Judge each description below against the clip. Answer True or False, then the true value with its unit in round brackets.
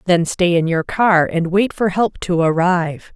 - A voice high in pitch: False (175 Hz)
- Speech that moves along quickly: True (210 wpm)